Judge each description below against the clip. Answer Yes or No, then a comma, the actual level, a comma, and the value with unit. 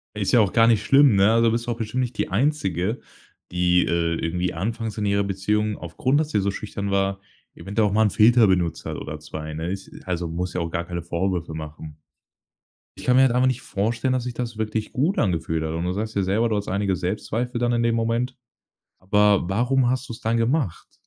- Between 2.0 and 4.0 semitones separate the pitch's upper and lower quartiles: No, average, 4.6 semitones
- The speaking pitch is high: No, low, 105 Hz